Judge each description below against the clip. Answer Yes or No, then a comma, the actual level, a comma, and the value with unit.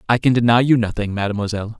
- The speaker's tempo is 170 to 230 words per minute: Yes, average, 200 wpm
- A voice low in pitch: Yes, low, 115 Hz